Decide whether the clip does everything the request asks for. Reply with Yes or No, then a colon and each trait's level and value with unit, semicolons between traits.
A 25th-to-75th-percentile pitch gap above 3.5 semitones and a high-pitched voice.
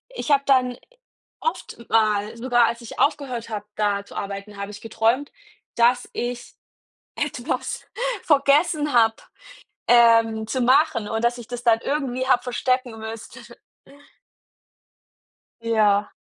No: average, 2.7 semitones; high, 235 Hz